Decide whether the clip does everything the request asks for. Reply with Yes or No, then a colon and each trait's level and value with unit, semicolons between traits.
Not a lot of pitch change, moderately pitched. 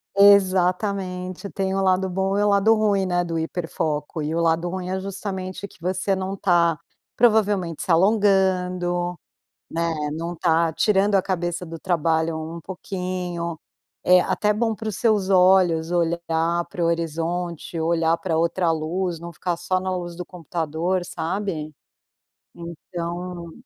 Yes: narrow, 2.2 semitones; medium, 180 Hz